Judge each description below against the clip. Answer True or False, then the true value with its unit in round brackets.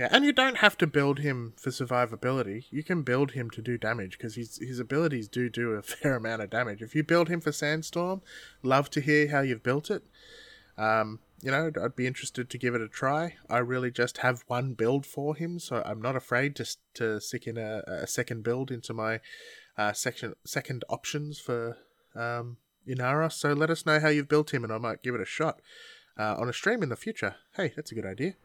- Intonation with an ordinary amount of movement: True (4.4 semitones)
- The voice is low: True (125 Hz)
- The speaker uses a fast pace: True (225 wpm)